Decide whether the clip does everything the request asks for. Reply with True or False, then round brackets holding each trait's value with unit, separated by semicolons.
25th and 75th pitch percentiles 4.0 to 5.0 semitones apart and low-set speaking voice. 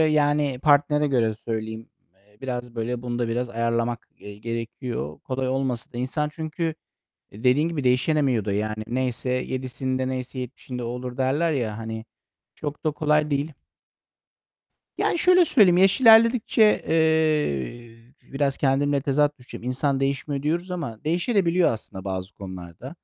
True (4.4 semitones; 130 Hz)